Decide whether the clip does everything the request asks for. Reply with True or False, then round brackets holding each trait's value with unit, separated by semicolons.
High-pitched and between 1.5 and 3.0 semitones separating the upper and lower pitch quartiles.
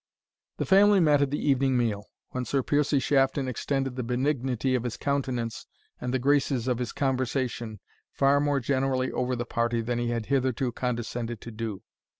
False (130 Hz; 2.5 semitones)